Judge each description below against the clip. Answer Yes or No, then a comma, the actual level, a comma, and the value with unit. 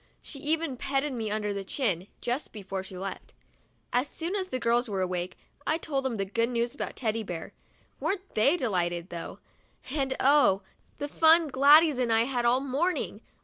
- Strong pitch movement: Yes, wide, 6.2 semitones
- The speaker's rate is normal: Yes, average, 185 wpm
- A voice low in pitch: No, high, 245 Hz